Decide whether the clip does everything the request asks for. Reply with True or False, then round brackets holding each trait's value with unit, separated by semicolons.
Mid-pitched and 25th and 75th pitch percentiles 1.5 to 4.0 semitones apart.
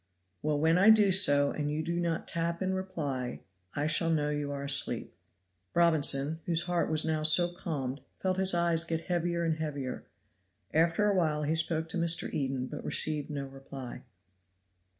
True (160 Hz; 2.9 semitones)